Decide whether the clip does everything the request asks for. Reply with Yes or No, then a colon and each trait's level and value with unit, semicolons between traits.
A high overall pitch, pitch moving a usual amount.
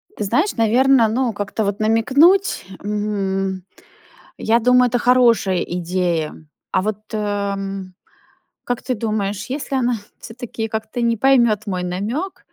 Yes: high, 220 Hz; average, 3.7 semitones